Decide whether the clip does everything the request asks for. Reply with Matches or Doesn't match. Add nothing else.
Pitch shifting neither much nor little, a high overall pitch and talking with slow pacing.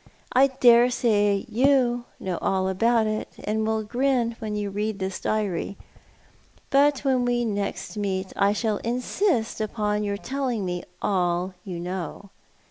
Doesn't match